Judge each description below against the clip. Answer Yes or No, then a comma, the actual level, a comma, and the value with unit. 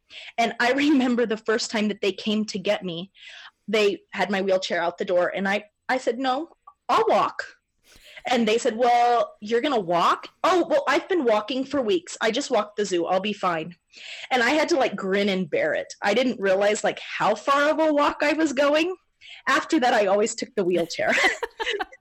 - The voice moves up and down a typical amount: No, wide, 6.6 semitones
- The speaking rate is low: No, fast, 205 wpm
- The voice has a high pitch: Yes, high, 235 Hz